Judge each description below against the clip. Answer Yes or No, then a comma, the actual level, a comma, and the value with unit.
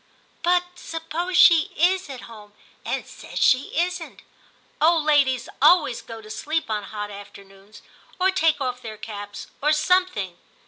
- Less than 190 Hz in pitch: No, very high, 290 Hz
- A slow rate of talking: No, average, 155 wpm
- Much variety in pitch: Yes, wide, 8.1 semitones